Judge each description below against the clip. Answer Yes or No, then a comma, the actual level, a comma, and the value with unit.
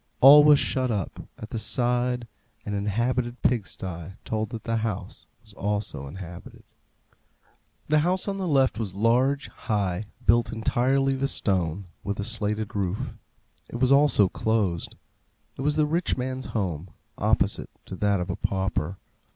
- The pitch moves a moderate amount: Yes, average, 4.8 semitones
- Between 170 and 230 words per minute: No, average, 155 wpm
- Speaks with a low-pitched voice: Yes, low, 110 Hz